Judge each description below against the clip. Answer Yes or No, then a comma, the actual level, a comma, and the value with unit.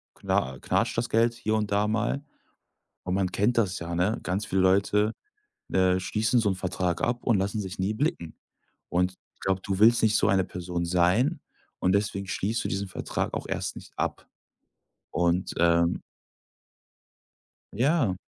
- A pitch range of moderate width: Yes, average, 3.2 semitones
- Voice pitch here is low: Yes, very low, 95 Hz